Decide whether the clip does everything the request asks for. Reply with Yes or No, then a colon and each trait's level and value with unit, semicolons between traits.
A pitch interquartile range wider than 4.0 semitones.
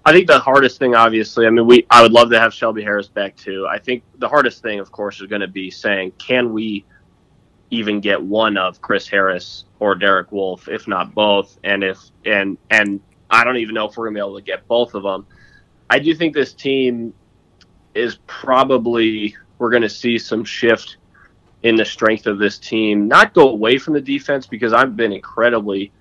No: average, 3.0 semitones